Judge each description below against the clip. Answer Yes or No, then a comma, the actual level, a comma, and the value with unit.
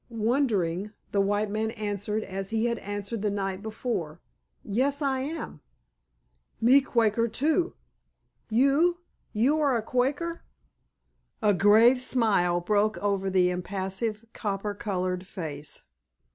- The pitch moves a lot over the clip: No, average, 4.0 semitones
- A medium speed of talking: No, slow, 115 wpm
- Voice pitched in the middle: No, high, 215 Hz